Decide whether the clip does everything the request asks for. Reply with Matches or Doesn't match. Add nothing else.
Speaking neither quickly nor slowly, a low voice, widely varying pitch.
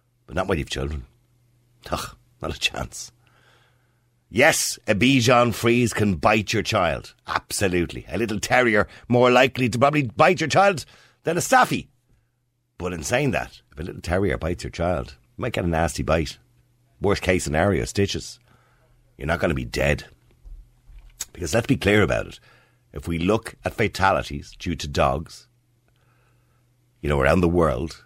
Matches